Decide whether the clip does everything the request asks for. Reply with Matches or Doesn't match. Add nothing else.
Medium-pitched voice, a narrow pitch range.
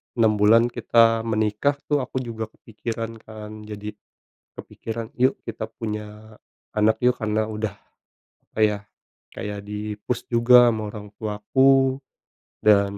Doesn't match